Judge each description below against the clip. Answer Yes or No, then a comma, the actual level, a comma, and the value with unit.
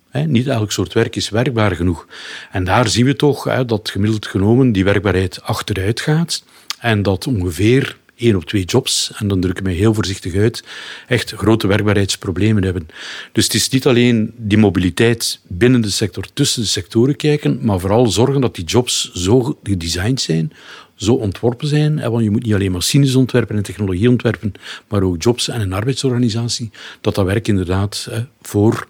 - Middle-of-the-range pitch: No, low, 110 Hz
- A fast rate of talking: No, average, 185 wpm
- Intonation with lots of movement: No, average, 3.7 semitones